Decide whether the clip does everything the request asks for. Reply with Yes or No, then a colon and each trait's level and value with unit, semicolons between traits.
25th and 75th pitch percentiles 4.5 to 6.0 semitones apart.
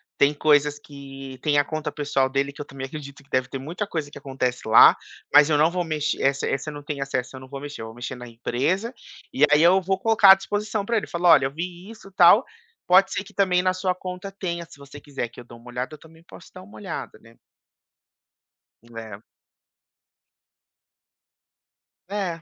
Yes: average, 5.1 semitones